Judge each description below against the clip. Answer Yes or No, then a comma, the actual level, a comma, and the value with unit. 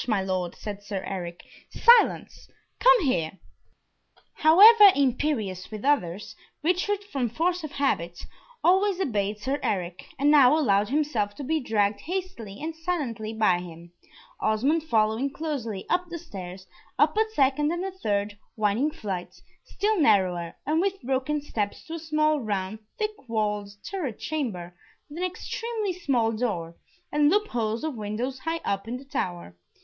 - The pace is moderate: Yes, average, 155 wpm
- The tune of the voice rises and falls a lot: Yes, wide, 7.8 semitones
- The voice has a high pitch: Yes, very high, 255 Hz